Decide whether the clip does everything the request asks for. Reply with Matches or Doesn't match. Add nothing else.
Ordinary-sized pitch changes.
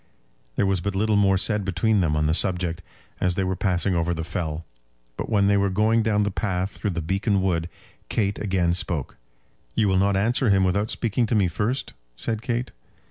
Matches